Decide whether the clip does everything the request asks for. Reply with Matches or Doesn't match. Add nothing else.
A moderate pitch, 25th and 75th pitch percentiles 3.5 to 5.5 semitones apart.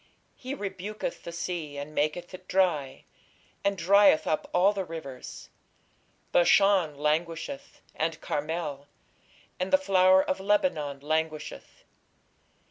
Matches